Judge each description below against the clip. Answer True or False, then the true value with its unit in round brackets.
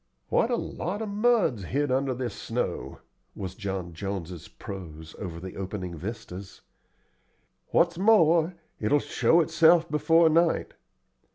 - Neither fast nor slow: False (130 wpm)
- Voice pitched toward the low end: True (130 Hz)